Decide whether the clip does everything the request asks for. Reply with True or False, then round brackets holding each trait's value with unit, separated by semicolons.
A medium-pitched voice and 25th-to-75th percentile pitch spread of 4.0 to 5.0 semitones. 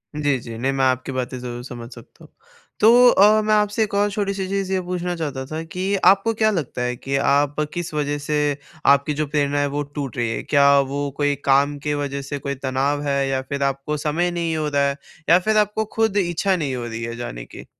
True (145 Hz; 4.7 semitones)